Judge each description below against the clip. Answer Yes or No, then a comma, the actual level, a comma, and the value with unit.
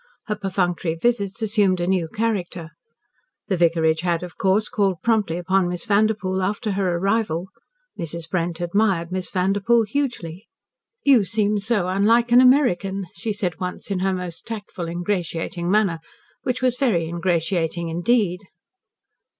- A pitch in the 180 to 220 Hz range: Yes, high, 190 Hz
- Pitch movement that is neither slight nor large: Yes, average, 3.6 semitones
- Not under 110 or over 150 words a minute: Yes, average, 140 wpm